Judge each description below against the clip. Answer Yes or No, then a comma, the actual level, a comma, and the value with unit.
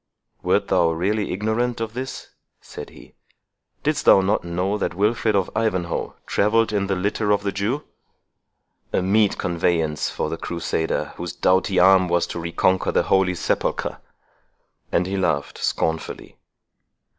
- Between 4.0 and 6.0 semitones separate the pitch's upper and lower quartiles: No, average, 3.4 semitones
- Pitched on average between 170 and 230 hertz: No, very low, 95 Hz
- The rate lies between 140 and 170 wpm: Yes, average, 145 wpm